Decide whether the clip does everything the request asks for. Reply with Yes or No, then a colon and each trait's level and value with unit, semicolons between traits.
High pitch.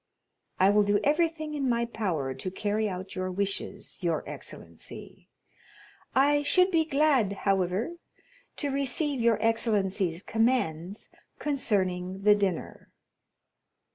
Yes: high, 210 Hz